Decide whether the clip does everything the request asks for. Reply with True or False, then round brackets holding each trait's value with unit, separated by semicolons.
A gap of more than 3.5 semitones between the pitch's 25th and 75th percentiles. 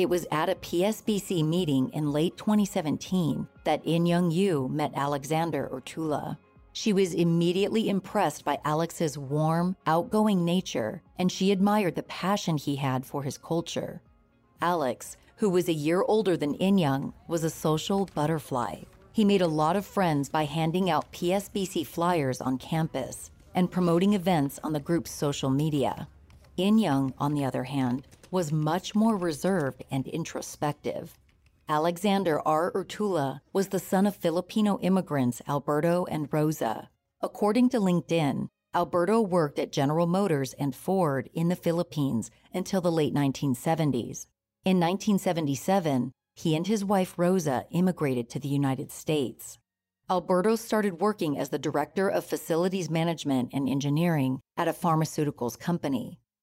True (4.6 semitones)